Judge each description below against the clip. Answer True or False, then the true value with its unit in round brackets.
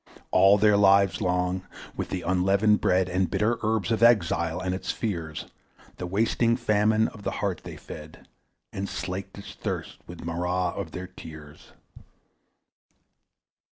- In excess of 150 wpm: False (145 wpm)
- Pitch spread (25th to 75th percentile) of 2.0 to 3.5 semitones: True (2.8 semitones)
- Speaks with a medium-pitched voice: False (95 Hz)